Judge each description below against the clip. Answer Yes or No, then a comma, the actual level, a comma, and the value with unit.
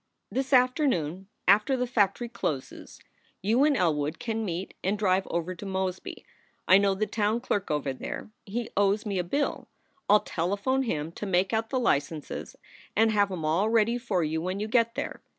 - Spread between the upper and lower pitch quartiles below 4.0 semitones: No, average, 4.4 semitones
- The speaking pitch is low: No, high, 200 Hz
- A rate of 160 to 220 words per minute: Yes, average, 185 wpm